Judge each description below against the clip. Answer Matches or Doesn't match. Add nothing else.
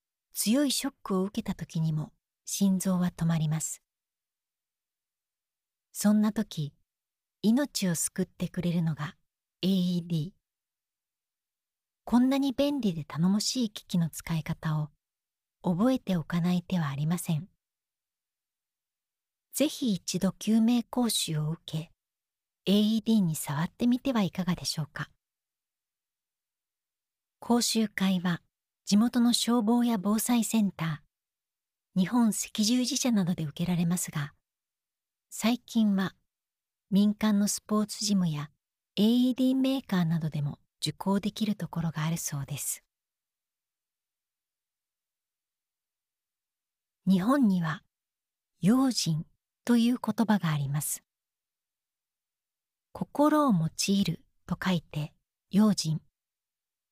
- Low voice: Doesn't match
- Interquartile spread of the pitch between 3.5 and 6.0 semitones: Matches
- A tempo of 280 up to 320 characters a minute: Doesn't match